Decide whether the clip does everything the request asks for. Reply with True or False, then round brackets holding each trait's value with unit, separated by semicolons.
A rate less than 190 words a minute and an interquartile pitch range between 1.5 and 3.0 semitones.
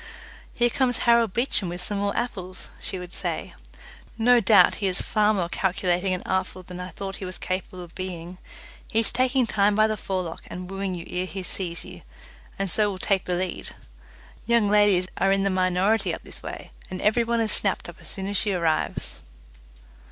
False (205 wpm; 2.7 semitones)